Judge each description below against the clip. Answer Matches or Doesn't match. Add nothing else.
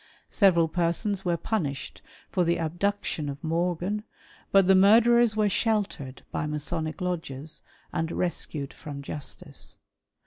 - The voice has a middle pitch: Matches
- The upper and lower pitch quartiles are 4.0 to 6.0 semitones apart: Matches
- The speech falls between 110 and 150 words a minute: Matches